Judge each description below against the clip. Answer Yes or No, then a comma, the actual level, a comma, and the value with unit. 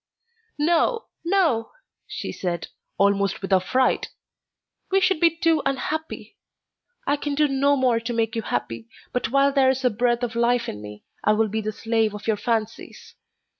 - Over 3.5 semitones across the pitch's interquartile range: Yes, average, 5.0 semitones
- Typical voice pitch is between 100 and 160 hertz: No, high, 240 Hz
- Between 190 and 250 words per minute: No, average, 170 wpm